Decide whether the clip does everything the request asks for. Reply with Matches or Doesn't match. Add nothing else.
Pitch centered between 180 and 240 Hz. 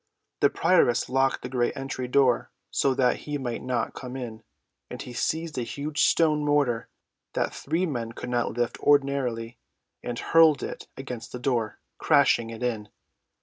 Doesn't match